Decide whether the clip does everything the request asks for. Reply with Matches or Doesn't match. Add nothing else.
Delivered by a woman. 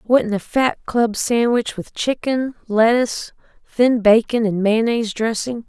Matches